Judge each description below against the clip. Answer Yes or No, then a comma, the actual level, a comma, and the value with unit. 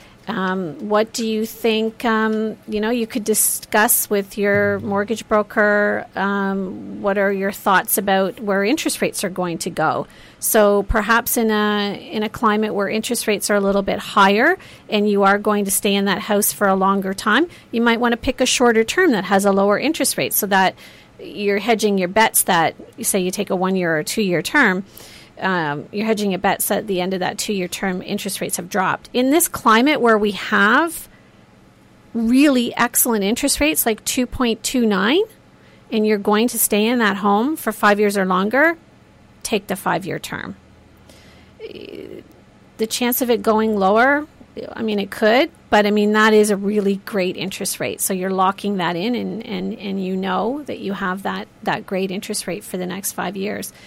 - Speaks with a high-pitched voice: Yes, high, 210 Hz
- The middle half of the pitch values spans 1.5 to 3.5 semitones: Yes, average, 2.8 semitones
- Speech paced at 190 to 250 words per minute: Yes, average, 195 wpm